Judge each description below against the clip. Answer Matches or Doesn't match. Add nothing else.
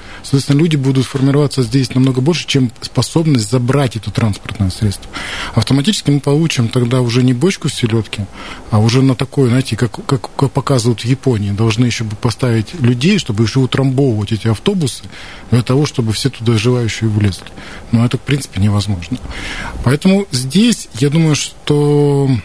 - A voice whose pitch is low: Matches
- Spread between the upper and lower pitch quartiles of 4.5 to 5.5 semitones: Doesn't match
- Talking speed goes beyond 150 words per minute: Matches